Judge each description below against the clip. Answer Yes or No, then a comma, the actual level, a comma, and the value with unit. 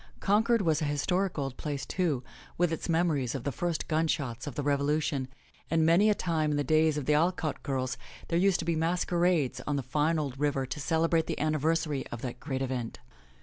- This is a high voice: No, medium, 155 Hz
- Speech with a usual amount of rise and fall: Yes, average, 3.3 semitones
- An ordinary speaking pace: No, fast, 215 wpm